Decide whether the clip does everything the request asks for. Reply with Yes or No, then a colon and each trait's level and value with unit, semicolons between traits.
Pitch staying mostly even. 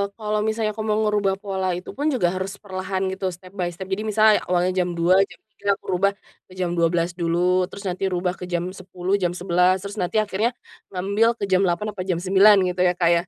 Yes: narrow, 2.2 semitones